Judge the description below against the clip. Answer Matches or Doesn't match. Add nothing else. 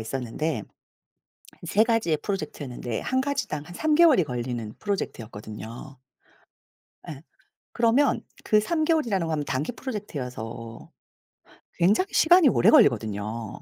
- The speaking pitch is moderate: Matches